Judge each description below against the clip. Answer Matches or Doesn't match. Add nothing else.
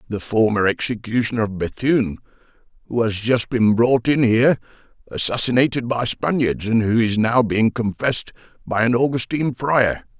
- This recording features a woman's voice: Doesn't match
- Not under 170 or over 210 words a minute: Doesn't match